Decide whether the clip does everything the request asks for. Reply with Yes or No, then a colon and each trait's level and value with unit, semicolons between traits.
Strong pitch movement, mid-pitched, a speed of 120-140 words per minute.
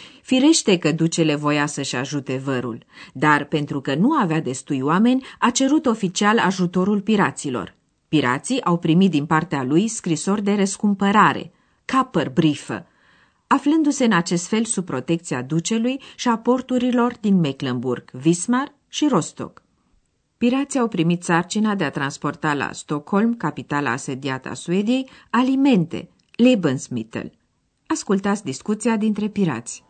Yes: wide, 8.0 semitones; medium, 175 Hz; average, 130 wpm